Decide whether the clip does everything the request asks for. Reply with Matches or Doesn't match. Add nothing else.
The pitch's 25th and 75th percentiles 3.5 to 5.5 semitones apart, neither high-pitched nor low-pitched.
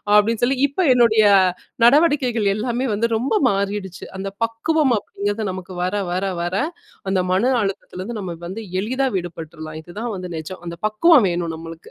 Doesn't match